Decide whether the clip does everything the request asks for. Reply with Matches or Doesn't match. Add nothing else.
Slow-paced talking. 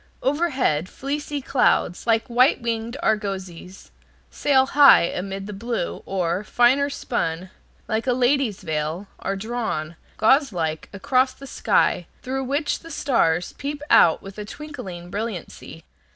Matches